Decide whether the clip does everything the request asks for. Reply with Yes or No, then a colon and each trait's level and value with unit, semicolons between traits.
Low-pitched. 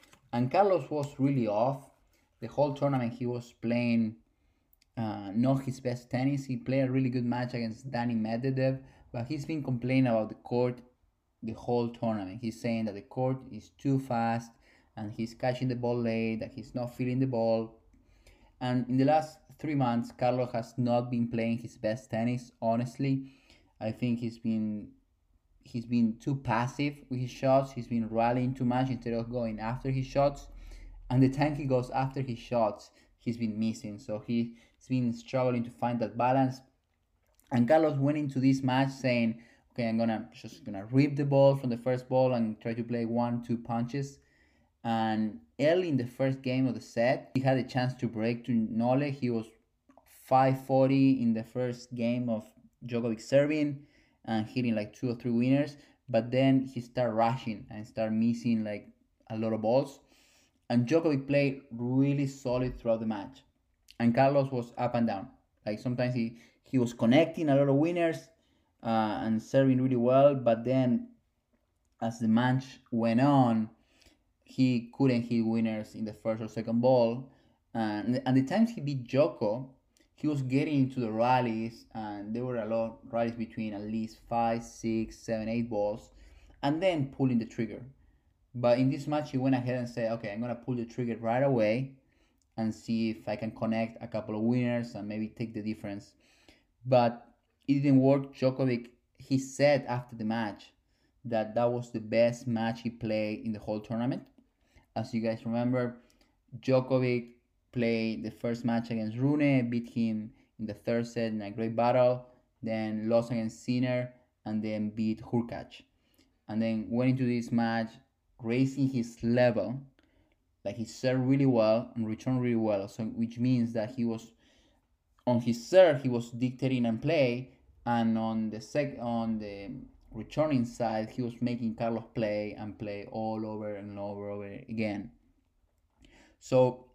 Yes: low, 120 Hz